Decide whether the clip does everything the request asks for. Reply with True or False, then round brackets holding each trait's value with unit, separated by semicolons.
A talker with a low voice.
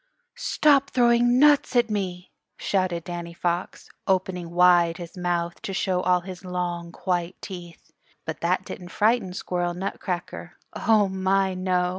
False (180 Hz)